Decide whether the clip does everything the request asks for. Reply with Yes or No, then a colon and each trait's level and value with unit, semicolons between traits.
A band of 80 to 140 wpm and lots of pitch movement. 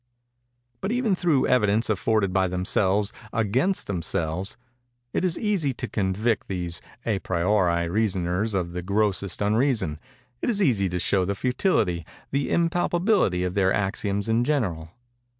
Yes: slow, 135 wpm; wide, 5.7 semitones